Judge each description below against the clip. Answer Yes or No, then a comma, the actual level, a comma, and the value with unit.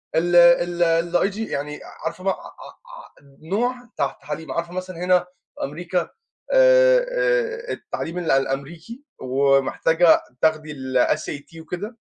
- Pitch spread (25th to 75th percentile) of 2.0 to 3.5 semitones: No, average, 3.9 semitones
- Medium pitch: Yes, medium, 175 Hz